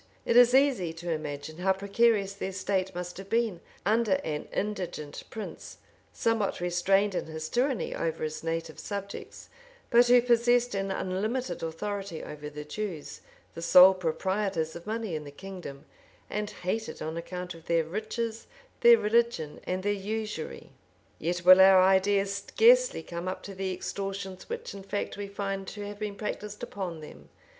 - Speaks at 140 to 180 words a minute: Yes, average, 165 wpm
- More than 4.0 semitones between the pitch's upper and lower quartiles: No, average, 3.7 semitones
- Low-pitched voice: No, high, 195 Hz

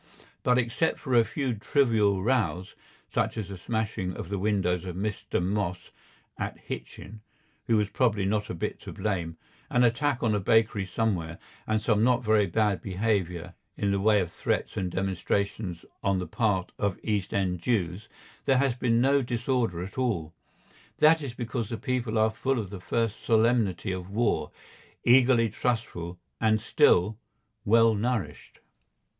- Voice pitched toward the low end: Yes, low, 105 Hz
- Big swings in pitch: No, average, 3.8 semitones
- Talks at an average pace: Yes, average, 160 wpm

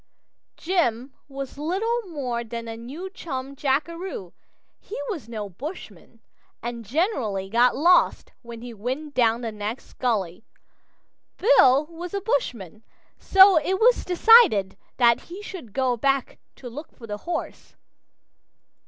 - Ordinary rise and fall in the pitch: No, wide, 6.9 semitones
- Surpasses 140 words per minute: No, slow, 135 wpm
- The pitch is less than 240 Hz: No, very high, 265 Hz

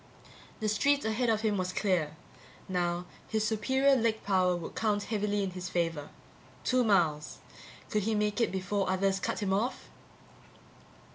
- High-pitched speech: Yes, high, 205 Hz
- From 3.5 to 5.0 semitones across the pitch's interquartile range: No, average, 3.1 semitones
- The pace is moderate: Yes, average, 160 wpm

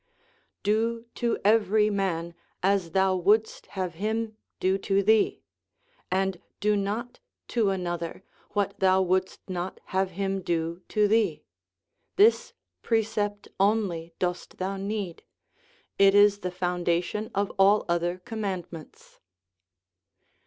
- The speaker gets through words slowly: Yes, slow, 115 wpm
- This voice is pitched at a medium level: No, high, 195 Hz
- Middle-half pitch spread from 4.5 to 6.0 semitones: No, narrow, 2.6 semitones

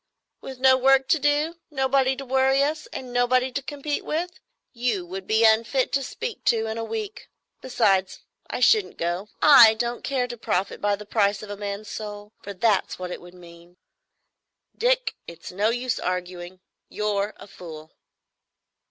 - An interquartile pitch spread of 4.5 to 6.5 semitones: Yes, average, 5.1 semitones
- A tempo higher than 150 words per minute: Yes, average, 170 wpm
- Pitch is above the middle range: Yes, high, 230 Hz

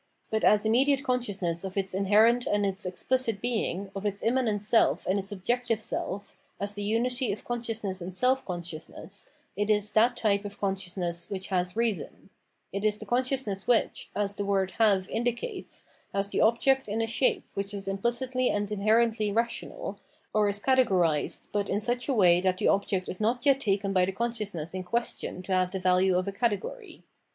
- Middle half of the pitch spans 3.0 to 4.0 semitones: Yes, average, 3.6 semitones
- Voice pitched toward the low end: No, high, 205 Hz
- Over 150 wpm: Yes, average, 190 wpm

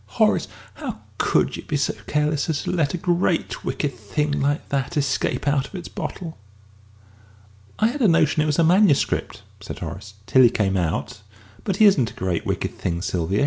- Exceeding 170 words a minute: Yes, average, 190 wpm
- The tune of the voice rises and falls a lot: Yes, wide, 7.3 semitones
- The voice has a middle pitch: Yes, medium, 145 Hz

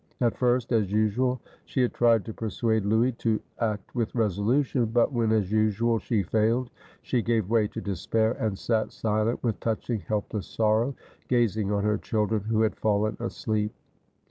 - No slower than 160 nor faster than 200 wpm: Yes, average, 170 wpm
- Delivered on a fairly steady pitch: Yes, narrow, 1.8 semitones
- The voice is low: Yes, low, 110 Hz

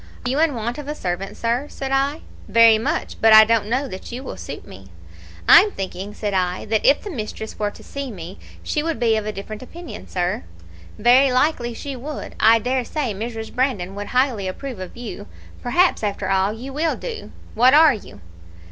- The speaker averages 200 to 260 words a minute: Yes, fast, 205 wpm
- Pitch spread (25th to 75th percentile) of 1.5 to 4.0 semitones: No, average, 4.8 semitones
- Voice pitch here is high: Yes, high, 230 Hz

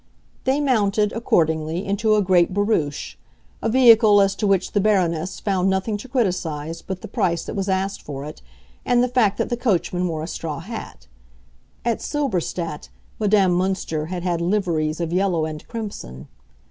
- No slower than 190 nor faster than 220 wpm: No, average, 165 wpm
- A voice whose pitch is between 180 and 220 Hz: Yes, high, 190 Hz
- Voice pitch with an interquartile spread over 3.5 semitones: Yes, average, 4.2 semitones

